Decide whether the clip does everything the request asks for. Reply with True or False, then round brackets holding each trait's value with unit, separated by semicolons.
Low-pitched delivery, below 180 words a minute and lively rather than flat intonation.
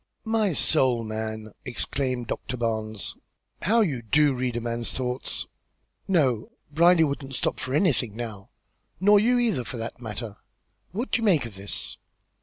True (125 Hz; 155 wpm; 6.6 semitones)